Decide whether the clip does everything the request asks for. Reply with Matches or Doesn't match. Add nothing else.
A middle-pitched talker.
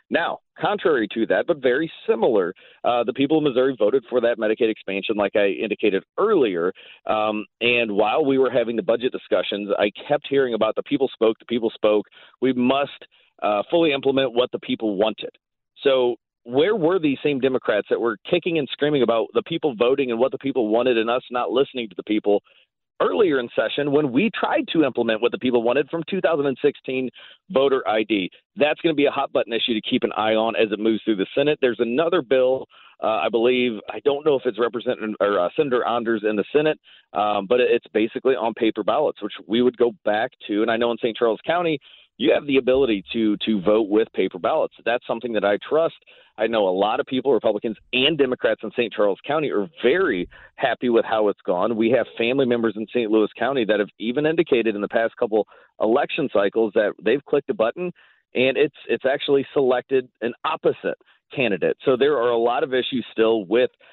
Doesn't match